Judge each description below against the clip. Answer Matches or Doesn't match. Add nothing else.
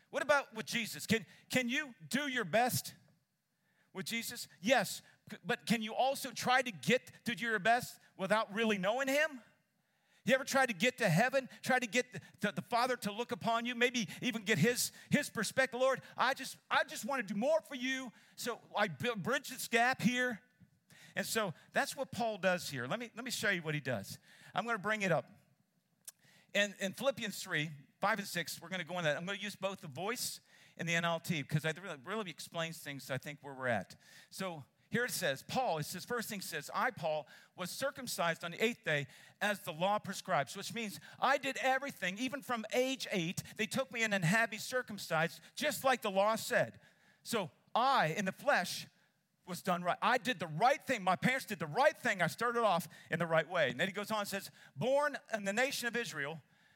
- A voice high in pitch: Matches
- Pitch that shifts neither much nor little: Doesn't match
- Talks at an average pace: Doesn't match